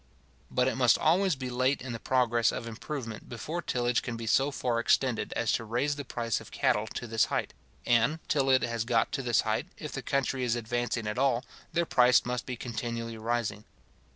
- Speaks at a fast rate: Yes, fast, 210 wpm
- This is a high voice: No, low, 120 Hz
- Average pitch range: No, narrow, 2.2 semitones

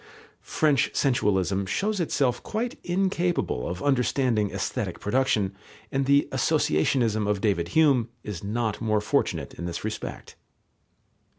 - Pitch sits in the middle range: No, low, 115 Hz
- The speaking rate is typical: No, slow, 120 wpm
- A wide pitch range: Yes, wide, 5.7 semitones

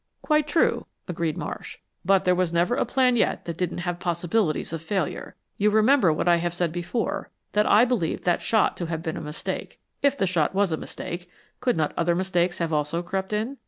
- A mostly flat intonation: No, average, 4.0 semitones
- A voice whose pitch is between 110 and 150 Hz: No, medium, 175 Hz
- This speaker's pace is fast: Yes, fast, 210 wpm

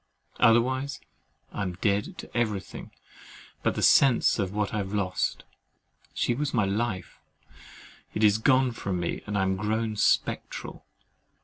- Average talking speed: Yes, average, 145 wpm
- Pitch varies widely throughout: No, average, 3.4 semitones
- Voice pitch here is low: Yes, low, 105 Hz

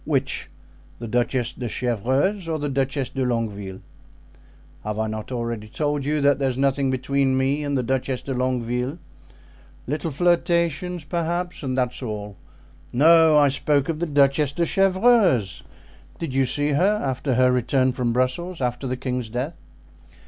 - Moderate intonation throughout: Yes, average, 3.4 semitones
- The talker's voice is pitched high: No, low, 135 Hz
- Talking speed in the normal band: Yes, average, 155 wpm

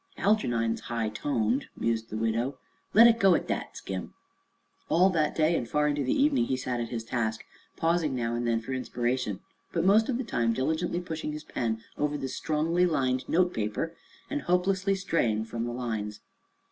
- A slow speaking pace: No, average, 185 wpm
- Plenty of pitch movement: Yes, wide, 7.0 semitones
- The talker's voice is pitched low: Yes, low, 130 Hz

